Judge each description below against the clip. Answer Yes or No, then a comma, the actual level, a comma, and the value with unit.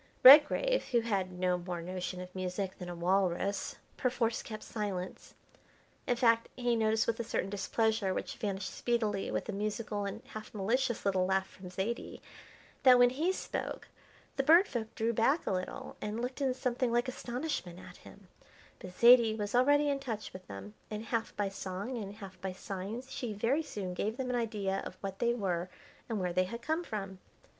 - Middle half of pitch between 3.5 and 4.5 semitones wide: Yes, average, 4.2 semitones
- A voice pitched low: No, high, 215 Hz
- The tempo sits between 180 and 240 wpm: Yes, average, 190 wpm